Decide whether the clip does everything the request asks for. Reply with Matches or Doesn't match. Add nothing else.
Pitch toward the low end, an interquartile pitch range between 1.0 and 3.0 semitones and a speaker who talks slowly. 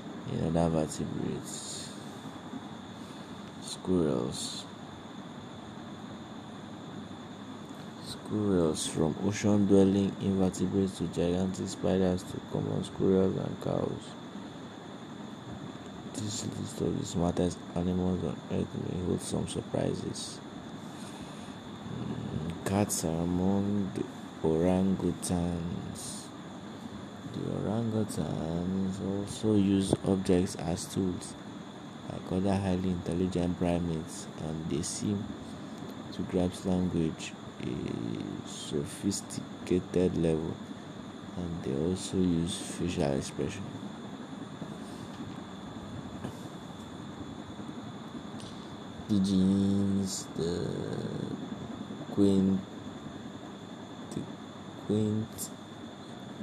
Matches